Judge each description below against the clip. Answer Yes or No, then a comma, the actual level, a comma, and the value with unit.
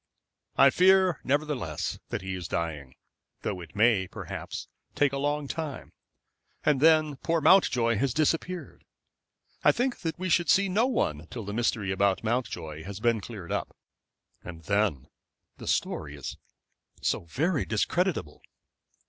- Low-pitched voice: Yes, low, 120 Hz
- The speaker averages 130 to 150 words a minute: Yes, average, 145 wpm